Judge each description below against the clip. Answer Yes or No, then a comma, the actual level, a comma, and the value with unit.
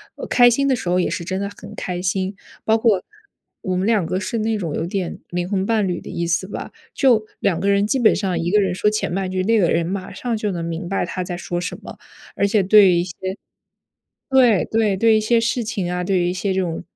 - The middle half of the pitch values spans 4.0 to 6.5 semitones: No, average, 3.3 semitones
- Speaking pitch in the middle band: No, high, 195 Hz